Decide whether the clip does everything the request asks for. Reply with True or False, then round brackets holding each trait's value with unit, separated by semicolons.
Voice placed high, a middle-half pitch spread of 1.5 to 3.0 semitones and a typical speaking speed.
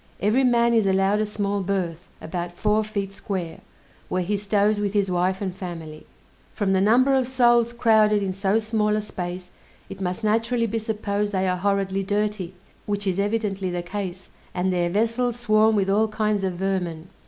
True (200 Hz; 2.4 semitones; 185 wpm)